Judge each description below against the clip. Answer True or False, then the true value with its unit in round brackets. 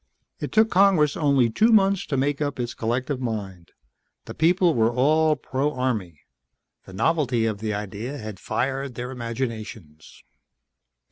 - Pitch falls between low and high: False (125 Hz)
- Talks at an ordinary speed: True (145 wpm)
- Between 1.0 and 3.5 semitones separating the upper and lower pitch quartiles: False (5.1 semitones)